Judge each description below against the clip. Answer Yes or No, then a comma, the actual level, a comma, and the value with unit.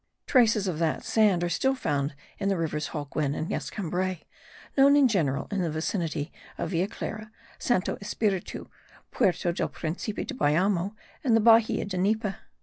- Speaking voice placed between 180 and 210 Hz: Yes, medium, 185 Hz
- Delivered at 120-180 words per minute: Yes, average, 160 wpm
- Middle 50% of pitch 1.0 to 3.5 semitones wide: No, average, 4.9 semitones